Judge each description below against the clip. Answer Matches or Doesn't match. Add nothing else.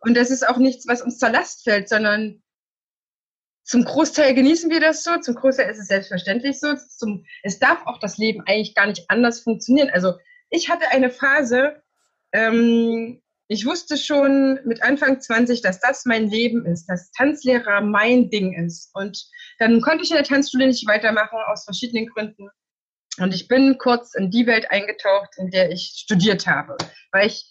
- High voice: Matches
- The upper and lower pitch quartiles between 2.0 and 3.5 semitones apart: Doesn't match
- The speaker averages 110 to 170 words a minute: Doesn't match